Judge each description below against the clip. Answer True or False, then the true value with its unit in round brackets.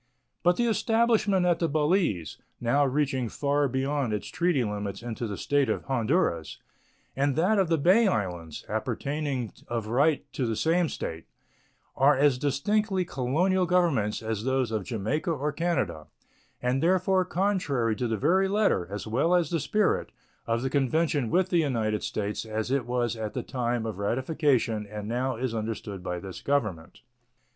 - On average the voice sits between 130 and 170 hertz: True (135 Hz)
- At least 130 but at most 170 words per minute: True (165 wpm)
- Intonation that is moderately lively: False (7.1 semitones)